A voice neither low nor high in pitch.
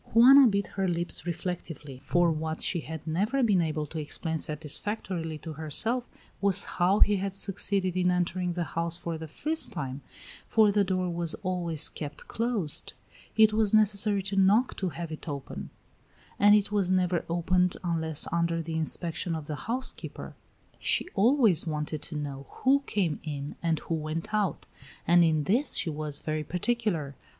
Yes: medium, 175 Hz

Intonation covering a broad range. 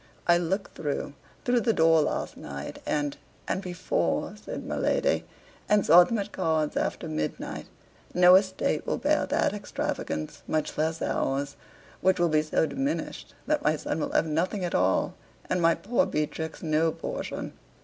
No: average, 4.3 semitones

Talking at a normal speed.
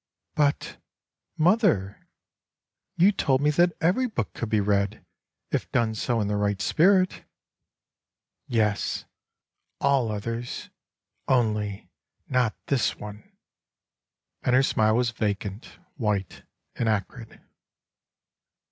No: slow, 115 wpm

